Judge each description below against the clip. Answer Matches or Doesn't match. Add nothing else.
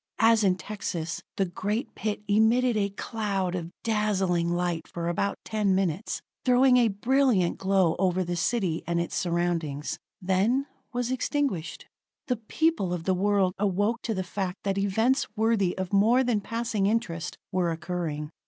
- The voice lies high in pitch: Matches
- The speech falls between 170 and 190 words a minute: Doesn't match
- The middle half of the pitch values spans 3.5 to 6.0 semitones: Matches